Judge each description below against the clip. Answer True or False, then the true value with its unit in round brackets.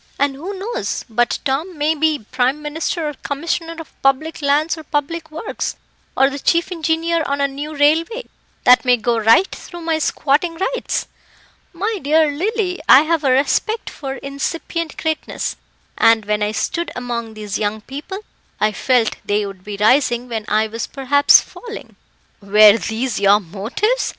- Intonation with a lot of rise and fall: True (6.0 semitones)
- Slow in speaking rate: False (165 wpm)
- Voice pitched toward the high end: True (285 Hz)